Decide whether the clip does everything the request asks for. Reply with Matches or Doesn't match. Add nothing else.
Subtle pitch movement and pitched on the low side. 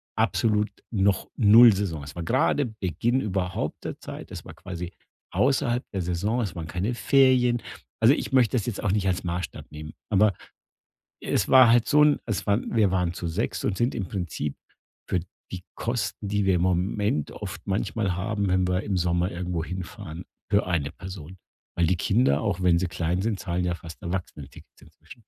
Doesn't match